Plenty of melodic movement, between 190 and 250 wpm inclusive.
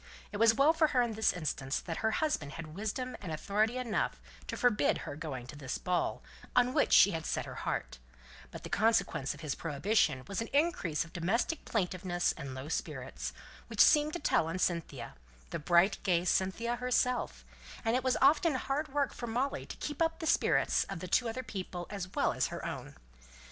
Yes: wide, 7.1 semitones; average, 200 wpm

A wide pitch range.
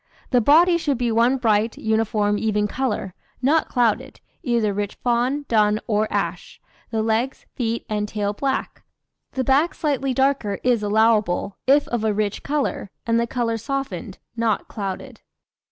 No: average, 3.9 semitones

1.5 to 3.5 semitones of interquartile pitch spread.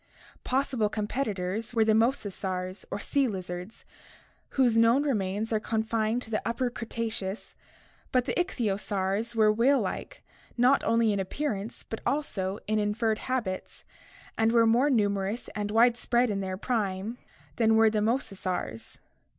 Yes: average, 2.9 semitones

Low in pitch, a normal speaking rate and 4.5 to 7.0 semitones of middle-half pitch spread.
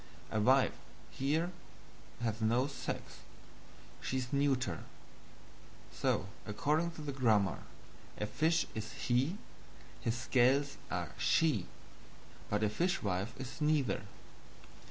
No: low, 130 Hz; slow, 110 wpm; average, 4.9 semitones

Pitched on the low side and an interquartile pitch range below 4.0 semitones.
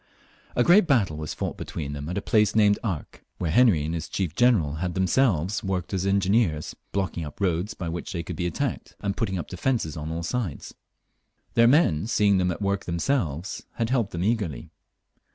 No: very low, 95 Hz; average, 4.7 semitones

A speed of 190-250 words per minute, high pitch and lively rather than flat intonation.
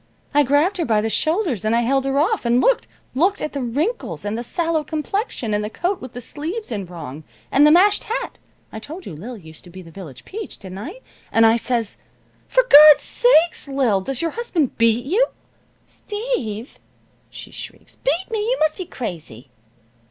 Yes: average, 195 wpm; very high, 275 Hz; wide, 8.3 semitones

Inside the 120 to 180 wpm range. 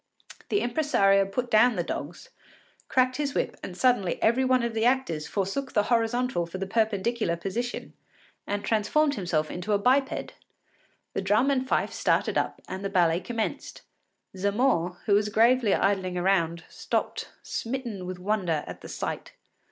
Yes: average, 160 wpm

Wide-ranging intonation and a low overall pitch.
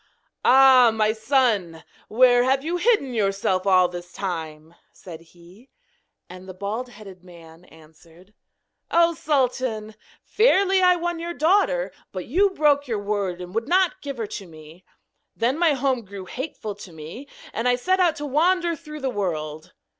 No: wide, 8.4 semitones; high, 230 Hz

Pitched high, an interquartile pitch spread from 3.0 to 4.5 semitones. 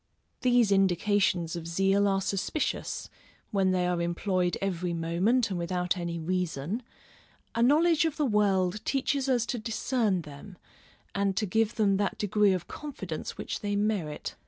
Yes: high, 195 Hz; average, 3.8 semitones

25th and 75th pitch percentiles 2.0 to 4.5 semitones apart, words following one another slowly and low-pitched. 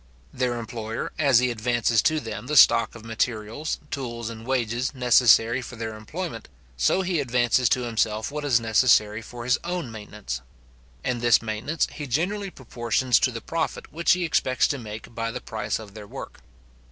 No: average, 2.9 semitones; average, 175 wpm; low, 120 Hz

